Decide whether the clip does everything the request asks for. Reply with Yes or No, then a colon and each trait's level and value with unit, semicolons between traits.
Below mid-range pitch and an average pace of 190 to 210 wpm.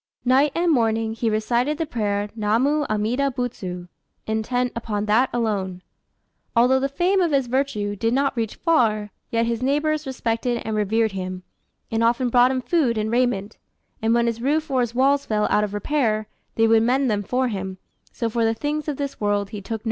No: high, 230 Hz; average, 200 wpm